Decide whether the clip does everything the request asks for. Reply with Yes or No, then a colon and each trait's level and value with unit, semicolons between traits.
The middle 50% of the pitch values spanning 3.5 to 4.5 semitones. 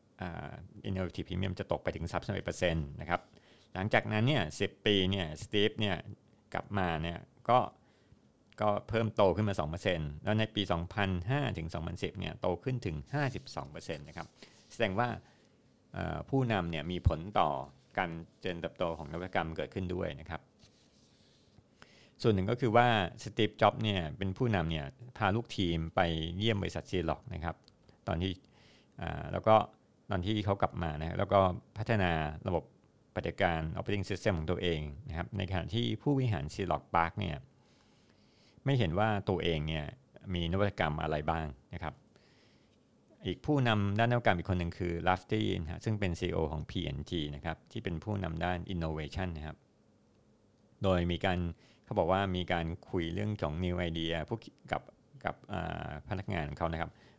Yes: average, 4.1 semitones